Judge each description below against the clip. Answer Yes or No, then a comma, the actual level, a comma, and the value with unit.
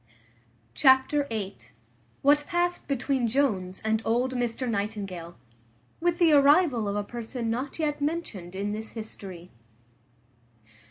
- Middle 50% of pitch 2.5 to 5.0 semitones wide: No, wide, 5.6 semitones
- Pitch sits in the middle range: No, high, 240 Hz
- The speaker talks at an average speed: No, slow, 120 wpm